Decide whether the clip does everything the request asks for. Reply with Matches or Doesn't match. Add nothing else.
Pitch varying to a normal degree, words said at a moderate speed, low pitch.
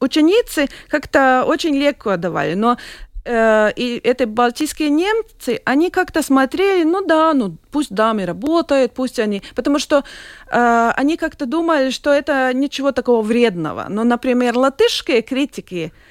Doesn't match